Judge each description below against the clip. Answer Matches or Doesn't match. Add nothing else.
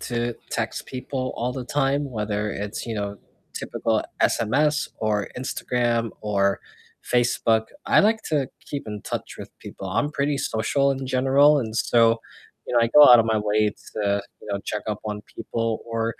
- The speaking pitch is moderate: Doesn't match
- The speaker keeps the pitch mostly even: Doesn't match